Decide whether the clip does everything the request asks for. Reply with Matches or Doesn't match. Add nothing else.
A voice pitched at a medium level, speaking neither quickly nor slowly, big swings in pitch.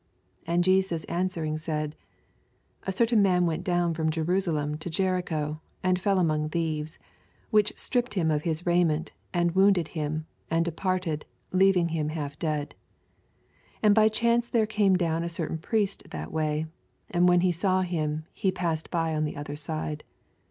Doesn't match